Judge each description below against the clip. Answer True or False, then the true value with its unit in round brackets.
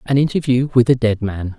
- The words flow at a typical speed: False (225 wpm)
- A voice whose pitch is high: False (120 Hz)